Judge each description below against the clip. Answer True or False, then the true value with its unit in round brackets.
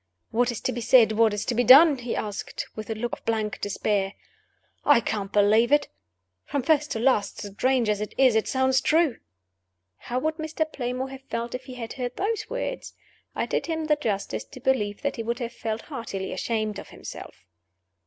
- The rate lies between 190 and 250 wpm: True (205 wpm)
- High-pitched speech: True (240 Hz)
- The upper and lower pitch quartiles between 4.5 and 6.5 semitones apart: False (3.7 semitones)